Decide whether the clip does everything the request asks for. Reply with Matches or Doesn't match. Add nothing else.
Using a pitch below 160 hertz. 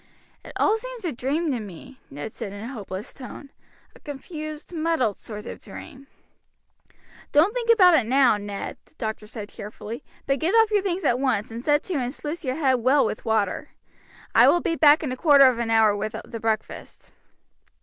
Doesn't match